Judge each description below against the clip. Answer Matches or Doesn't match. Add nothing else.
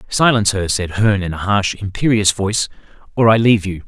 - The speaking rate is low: Doesn't match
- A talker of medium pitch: Doesn't match